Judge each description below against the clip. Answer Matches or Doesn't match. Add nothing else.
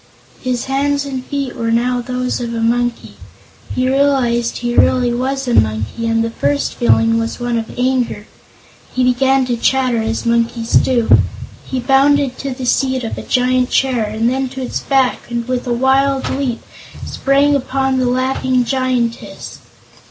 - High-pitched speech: Matches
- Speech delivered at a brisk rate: Doesn't match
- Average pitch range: Doesn't match